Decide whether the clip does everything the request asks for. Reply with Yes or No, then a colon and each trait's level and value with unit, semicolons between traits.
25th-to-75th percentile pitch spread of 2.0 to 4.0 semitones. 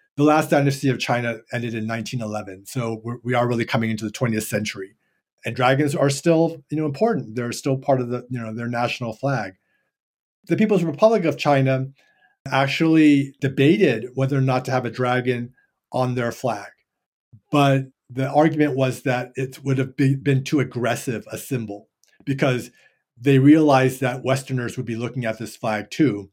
Yes: average, 3.1 semitones